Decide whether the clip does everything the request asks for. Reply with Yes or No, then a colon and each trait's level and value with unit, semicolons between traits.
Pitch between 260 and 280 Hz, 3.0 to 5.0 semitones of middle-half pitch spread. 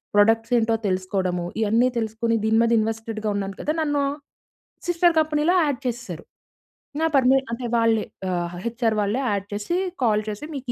No: high, 225 Hz; average, 3.7 semitones